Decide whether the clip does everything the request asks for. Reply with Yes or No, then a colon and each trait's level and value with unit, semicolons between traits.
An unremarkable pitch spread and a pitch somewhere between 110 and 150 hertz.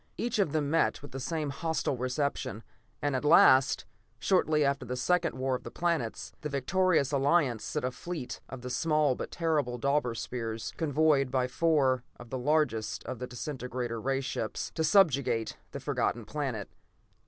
Yes: average, 3.7 semitones; medium, 140 Hz